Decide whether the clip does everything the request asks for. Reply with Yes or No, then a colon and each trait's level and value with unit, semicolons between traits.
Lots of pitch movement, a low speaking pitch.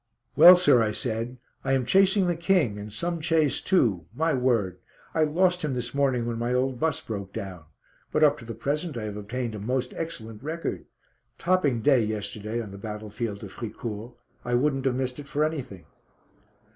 Yes: wide, 5.8 semitones; low, 125 Hz